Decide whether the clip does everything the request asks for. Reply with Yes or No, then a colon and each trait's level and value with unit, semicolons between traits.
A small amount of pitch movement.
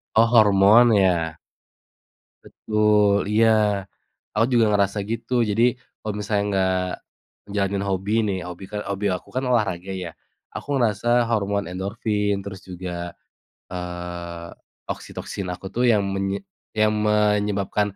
Yes: narrow, 2.3 semitones